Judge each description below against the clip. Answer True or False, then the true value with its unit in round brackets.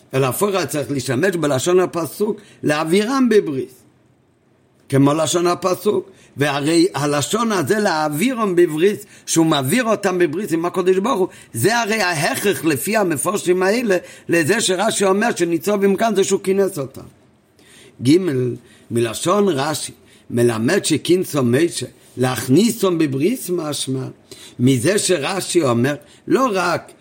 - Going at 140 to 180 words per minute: False (120 wpm)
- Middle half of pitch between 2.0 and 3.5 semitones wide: False (5.6 semitones)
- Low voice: False (175 Hz)